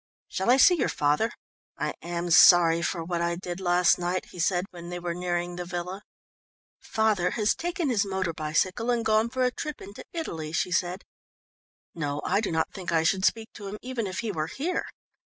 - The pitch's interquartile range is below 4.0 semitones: No, average, 4.3 semitones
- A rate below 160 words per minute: No, fast, 205 wpm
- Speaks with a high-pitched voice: No, medium, 180 Hz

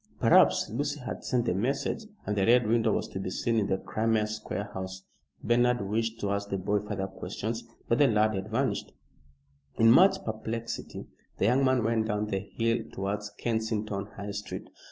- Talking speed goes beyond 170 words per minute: Yes, average, 185 wpm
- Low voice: Yes, low, 110 Hz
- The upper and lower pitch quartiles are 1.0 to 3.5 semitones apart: Yes, narrow, 2.5 semitones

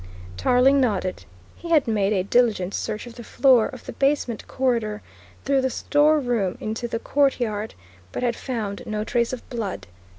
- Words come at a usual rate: Yes, average, 170 wpm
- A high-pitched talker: Yes, high, 235 Hz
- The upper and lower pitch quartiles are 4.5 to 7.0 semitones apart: No, average, 3.6 semitones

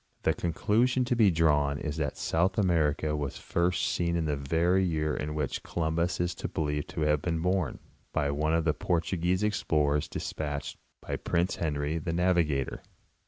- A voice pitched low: Yes, very low, 80 Hz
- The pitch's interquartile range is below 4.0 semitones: Yes, average, 2.8 semitones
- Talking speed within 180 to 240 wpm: No, average, 165 wpm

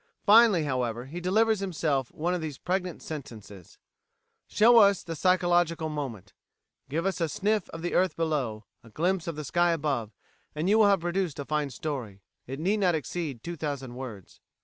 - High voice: No, medium, 160 Hz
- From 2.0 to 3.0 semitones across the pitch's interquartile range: No, average, 5.3 semitones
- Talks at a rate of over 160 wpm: Yes, average, 175 wpm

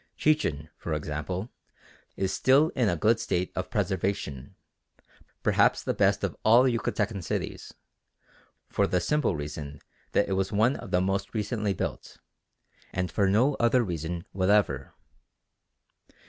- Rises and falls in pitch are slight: No, average, 4.6 semitones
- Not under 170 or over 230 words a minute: No, slow, 135 wpm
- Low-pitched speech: Yes, very low, 95 Hz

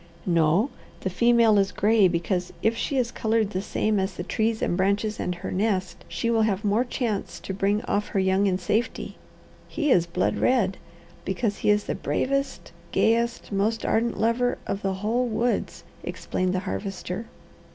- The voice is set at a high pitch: Yes, high, 210 Hz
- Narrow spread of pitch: No, average, 3.3 semitones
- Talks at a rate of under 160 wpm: No, average, 175 wpm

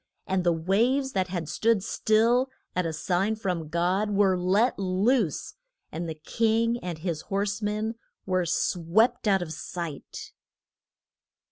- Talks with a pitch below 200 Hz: Yes, high, 190 Hz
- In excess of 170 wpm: No, average, 140 wpm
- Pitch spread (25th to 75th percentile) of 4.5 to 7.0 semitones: No, average, 4.0 semitones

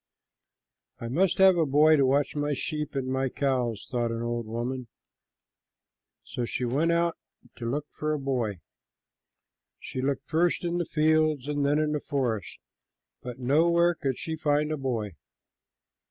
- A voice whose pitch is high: No, medium, 140 Hz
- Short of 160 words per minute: No, average, 165 wpm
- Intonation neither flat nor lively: Yes, average, 3.9 semitones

